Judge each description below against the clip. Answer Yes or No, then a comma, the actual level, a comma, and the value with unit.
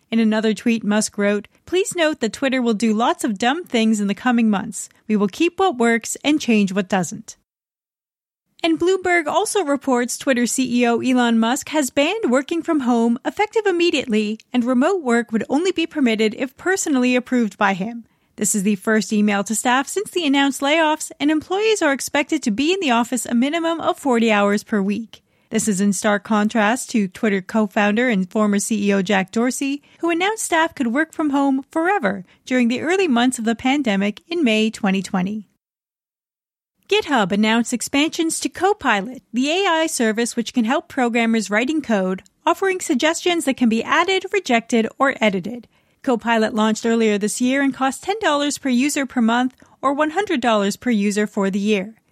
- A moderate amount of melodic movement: No, wide, 6.0 semitones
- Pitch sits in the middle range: No, high, 245 Hz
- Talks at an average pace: Yes, average, 180 wpm